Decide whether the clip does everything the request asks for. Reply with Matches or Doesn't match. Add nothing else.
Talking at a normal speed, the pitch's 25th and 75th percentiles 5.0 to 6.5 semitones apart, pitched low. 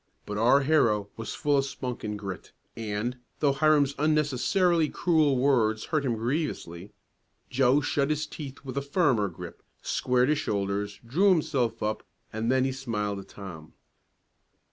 Matches